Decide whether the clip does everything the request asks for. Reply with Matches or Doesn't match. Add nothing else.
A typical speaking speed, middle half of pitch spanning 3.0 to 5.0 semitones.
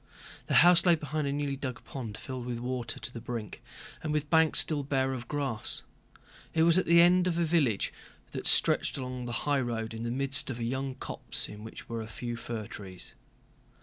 Doesn't match